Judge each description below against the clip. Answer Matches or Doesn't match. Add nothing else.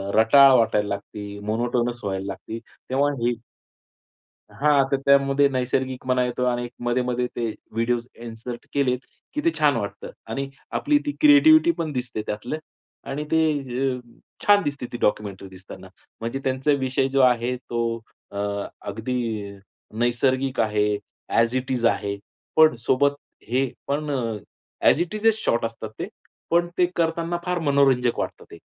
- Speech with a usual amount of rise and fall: Matches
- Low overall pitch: Matches